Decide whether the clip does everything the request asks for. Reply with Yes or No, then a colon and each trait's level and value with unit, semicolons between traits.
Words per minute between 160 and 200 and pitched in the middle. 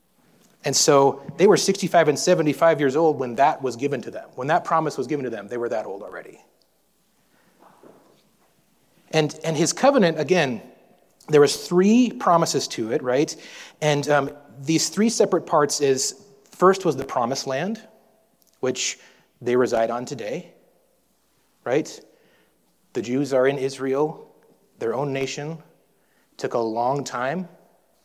No: average, 150 wpm; medium, 150 Hz